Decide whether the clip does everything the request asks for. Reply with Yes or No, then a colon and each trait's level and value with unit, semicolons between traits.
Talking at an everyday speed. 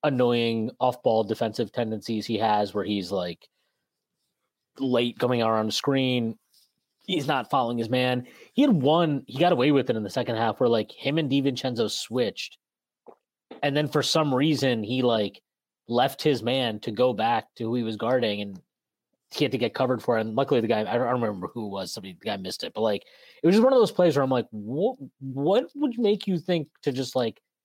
No: fast, 215 wpm